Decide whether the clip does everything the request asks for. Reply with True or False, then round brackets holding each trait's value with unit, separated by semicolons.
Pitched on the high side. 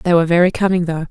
False (175 Hz)